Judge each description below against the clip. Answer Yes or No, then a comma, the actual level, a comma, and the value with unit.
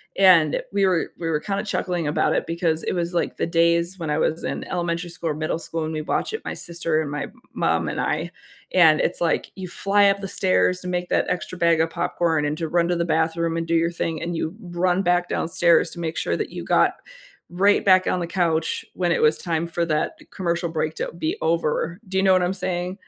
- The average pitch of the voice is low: No, medium, 170 Hz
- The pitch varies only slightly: Yes, narrow, 1.9 semitones